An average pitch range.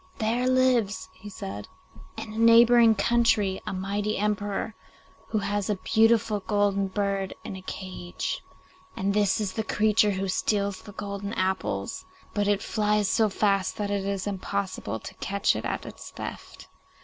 No: narrow, 1.8 semitones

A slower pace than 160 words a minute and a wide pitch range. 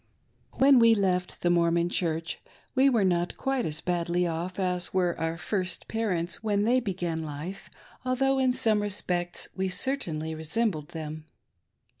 No: average, 150 wpm; average, 4.9 semitones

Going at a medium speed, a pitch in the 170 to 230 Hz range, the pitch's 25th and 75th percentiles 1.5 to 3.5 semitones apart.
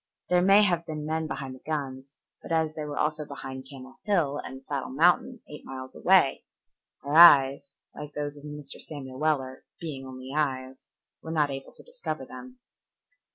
No: average, 175 wpm; medium, 145 Hz; average, 3.2 semitones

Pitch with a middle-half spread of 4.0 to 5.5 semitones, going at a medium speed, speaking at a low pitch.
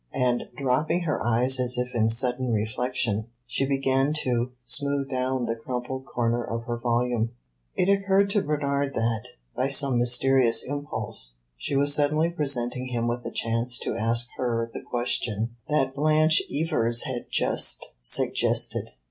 No: average, 2.9 semitones; average, 150 wpm; low, 125 Hz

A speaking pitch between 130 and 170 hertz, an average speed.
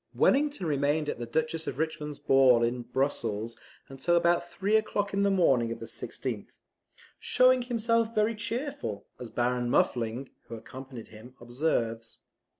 Yes: medium, 140 Hz; average, 150 wpm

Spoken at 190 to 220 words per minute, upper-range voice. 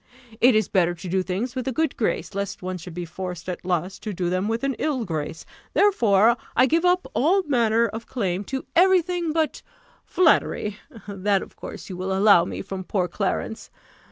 Yes: average, 200 wpm; high, 210 Hz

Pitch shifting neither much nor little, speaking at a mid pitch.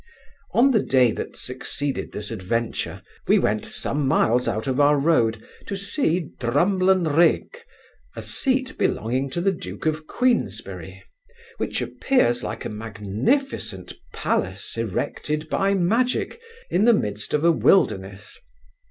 No: wide, 9.0 semitones; medium, 145 Hz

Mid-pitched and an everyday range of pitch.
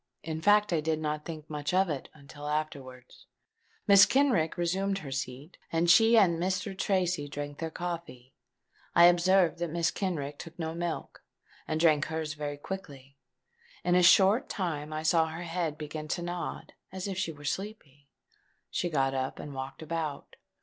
Yes: medium, 160 Hz; average, 3.3 semitones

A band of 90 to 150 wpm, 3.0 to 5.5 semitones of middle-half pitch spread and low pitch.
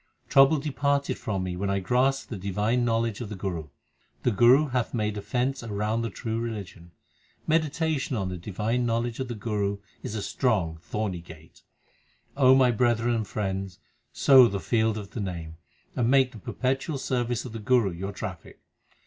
No: average, 185 wpm; average, 4.2 semitones; low, 115 Hz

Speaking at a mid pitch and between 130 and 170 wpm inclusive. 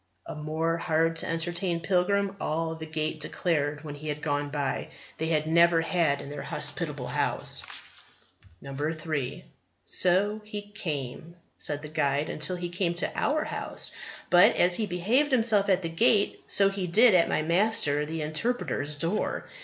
Yes: medium, 165 Hz; average, 160 wpm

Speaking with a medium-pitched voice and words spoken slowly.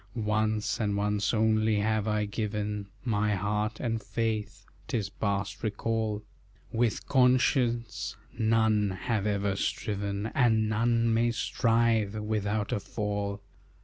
No: low, 110 Hz; slow, 115 wpm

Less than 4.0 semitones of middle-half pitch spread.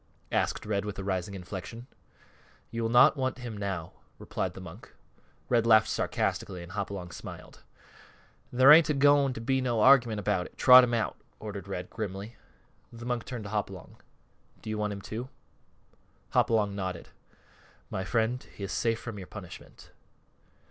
Yes: average, 3.6 semitones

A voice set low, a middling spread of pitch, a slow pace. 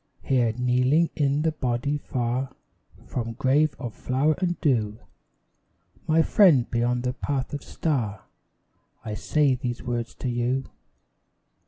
Yes: low, 130 Hz; average, 3.2 semitones; slow, 130 wpm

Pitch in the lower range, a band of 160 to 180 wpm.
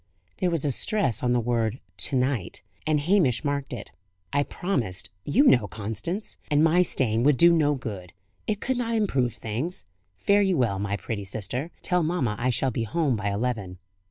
No: low, 130 Hz; average, 190 wpm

